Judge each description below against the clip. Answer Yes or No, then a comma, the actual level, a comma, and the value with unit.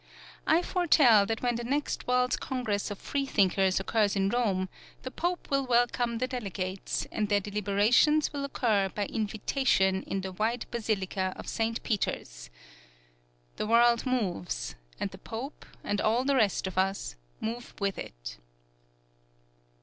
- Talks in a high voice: Yes, high, 220 Hz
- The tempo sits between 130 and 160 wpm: Yes, average, 145 wpm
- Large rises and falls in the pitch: No, average, 4.3 semitones